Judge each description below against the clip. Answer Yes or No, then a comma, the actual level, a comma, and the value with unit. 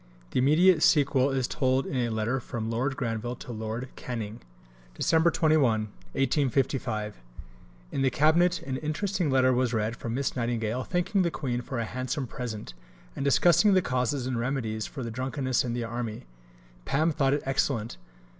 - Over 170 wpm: No, average, 165 wpm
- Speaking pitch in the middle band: No, low, 130 Hz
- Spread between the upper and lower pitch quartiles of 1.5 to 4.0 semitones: Yes, average, 3.4 semitones